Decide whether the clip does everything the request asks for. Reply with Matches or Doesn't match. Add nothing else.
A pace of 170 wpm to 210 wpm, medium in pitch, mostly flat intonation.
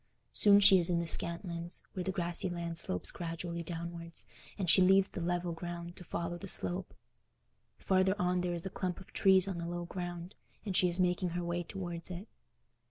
Matches